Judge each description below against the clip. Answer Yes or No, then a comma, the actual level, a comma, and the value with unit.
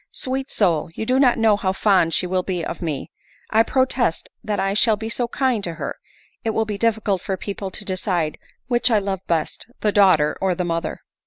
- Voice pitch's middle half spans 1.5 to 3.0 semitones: No, average, 3.8 semitones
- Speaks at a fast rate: Yes, fast, 215 wpm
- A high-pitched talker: Yes, high, 200 Hz